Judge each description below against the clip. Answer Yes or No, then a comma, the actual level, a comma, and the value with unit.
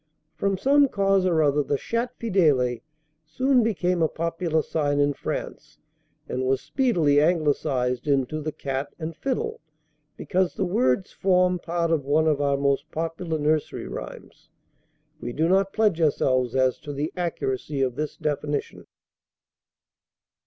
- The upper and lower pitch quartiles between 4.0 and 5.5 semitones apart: Yes, average, 4.4 semitones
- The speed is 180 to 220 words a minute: No, average, 145 wpm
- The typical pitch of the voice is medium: Yes, medium, 155 Hz